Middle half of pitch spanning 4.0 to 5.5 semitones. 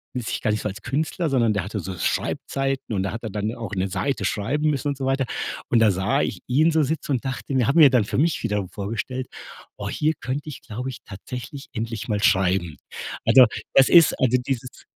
Yes: average, 4.8 semitones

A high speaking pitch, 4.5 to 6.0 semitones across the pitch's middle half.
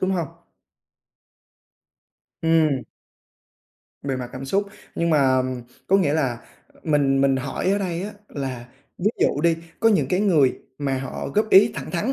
No: medium, 150 Hz; wide, 5.6 semitones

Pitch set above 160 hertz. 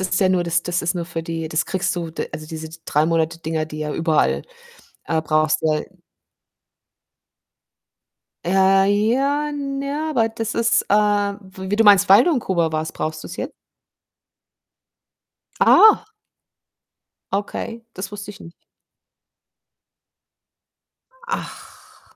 Yes: medium, 185 Hz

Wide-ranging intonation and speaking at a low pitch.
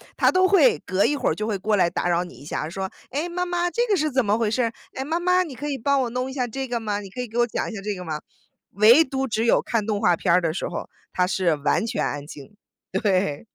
No: wide, 6.2 semitones; high, 225 Hz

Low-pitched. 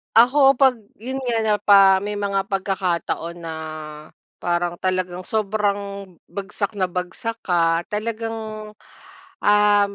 No: high, 200 Hz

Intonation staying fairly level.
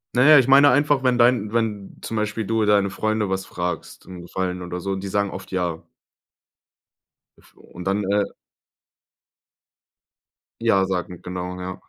No: average, 3.6 semitones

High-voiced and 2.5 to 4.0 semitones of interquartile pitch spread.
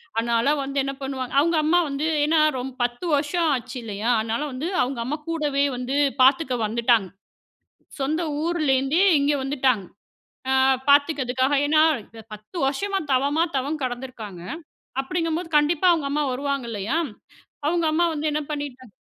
Yes: very high, 275 Hz; average, 3.7 semitones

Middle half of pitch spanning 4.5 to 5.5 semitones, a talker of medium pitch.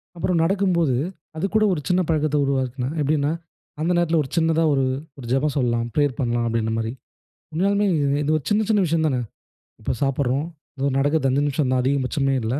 No: average, 3.9 semitones; medium, 145 Hz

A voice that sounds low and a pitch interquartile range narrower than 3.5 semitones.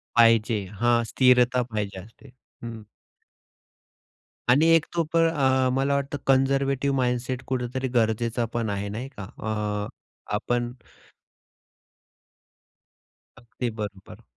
Yes: low, 120 Hz; average, 3.0 semitones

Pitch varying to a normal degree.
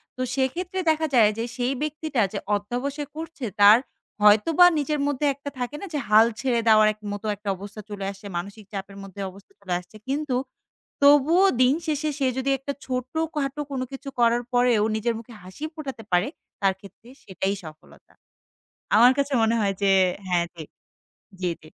No: wide, 5.8 semitones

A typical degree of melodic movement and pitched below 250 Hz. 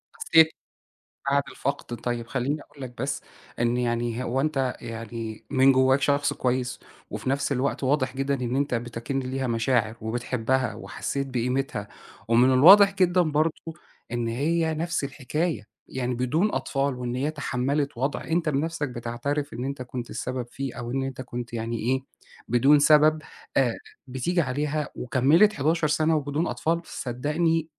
Yes: average, 3.4 semitones; low, 135 Hz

